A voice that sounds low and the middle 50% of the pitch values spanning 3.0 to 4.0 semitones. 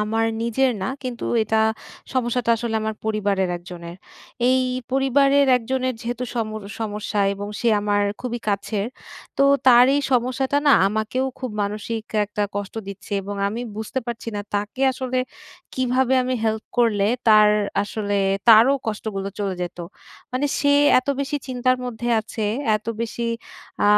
No: high, 225 Hz; average, 3.5 semitones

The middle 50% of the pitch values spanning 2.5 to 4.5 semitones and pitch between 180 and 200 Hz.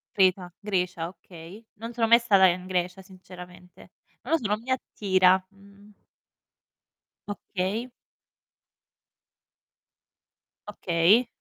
Yes: average, 2.8 semitones; high, 190 Hz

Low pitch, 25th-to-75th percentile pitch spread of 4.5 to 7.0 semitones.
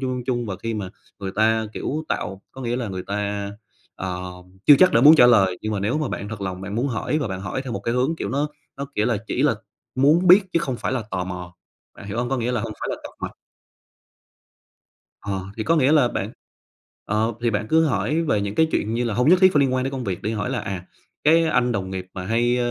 Yes: low, 115 Hz; average, 5.0 semitones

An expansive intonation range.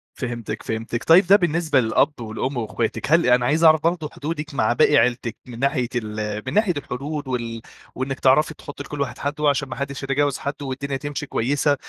No: average, 3.7 semitones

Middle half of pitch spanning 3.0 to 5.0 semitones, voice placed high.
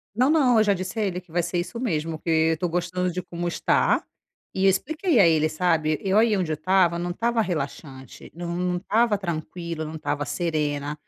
No: average, 3.5 semitones; medium, 175 Hz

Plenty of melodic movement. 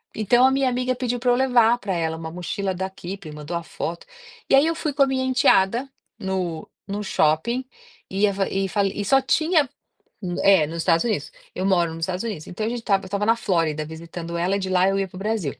Yes: wide, 5.9 semitones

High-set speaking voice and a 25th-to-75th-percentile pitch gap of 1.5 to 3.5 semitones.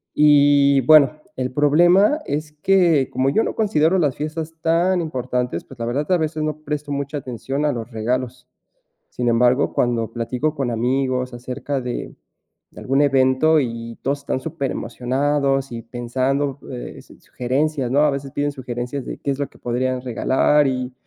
No: low, 135 Hz; average, 3.0 semitones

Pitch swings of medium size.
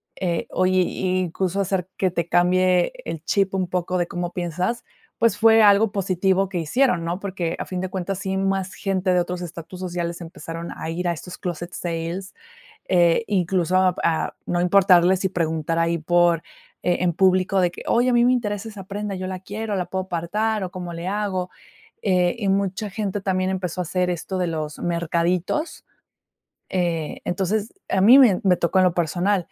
No: narrow, 2.0 semitones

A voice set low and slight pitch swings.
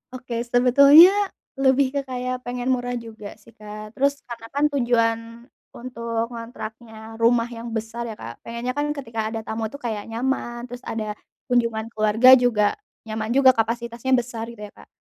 No: high, 235 Hz; narrow, 1.9 semitones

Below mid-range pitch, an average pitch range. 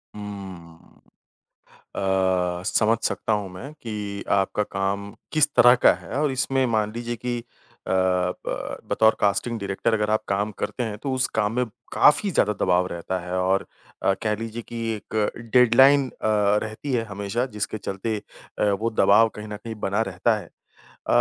Yes: low, 105 Hz; average, 3.3 semitones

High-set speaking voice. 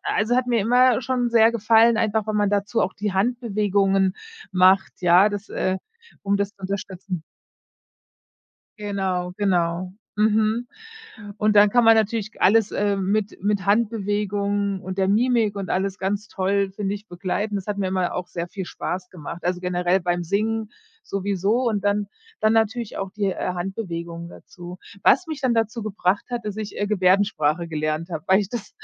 Yes: high, 200 Hz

